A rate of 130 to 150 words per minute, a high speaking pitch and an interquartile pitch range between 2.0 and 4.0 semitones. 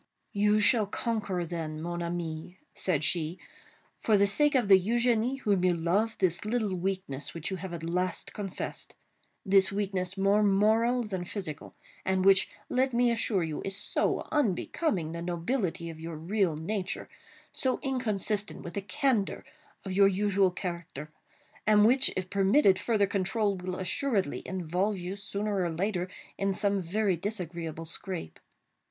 Yes: average, 145 wpm; high, 195 Hz; average, 3.2 semitones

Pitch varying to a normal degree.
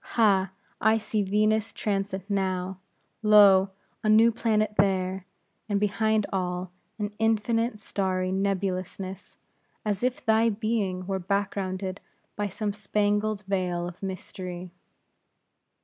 No: narrow, 2.2 semitones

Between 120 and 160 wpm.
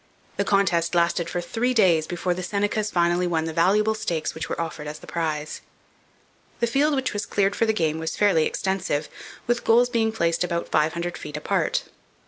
No: average, 195 wpm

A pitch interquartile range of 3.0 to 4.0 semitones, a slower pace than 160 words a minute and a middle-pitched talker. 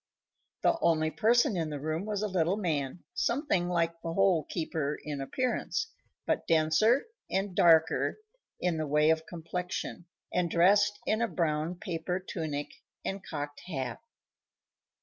Yes: average, 3.7 semitones; average, 145 wpm; medium, 170 Hz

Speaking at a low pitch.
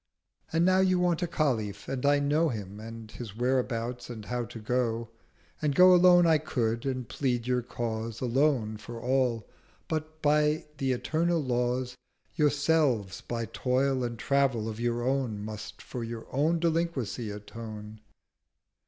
Yes: low, 125 Hz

